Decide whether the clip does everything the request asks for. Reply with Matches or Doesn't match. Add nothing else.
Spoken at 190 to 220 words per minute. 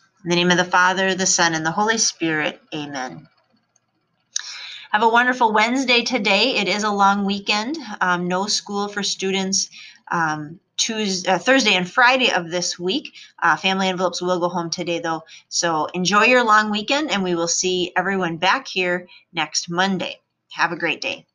Doesn't match